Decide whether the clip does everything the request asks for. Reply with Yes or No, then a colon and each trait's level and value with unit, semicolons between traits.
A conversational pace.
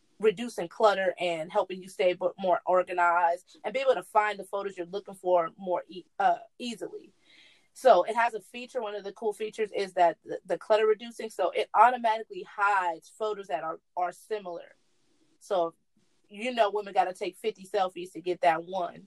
Yes: average, 190 wpm